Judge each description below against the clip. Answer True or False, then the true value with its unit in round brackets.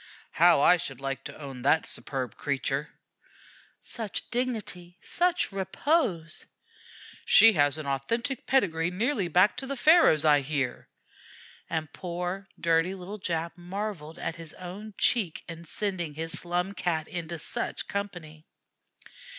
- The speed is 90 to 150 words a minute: True (135 wpm)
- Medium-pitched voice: True (175 Hz)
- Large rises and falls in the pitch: False (4.4 semitones)